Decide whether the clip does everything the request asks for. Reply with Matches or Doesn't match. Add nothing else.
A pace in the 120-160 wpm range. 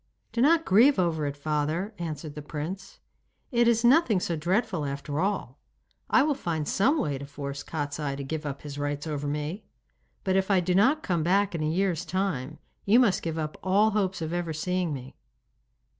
Doesn't match